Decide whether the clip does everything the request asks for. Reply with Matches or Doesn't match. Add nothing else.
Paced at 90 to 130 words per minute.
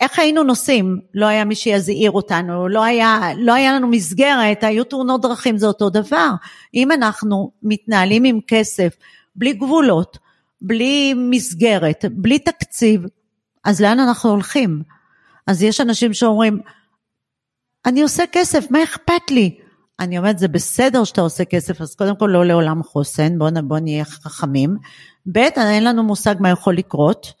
Doesn't match